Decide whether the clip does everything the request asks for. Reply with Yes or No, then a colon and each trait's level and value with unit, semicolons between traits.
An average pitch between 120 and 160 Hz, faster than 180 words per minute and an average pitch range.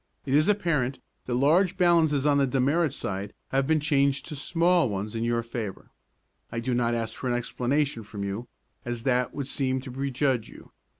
Yes: low, 135 Hz; average, 190 wpm; average, 3.9 semitones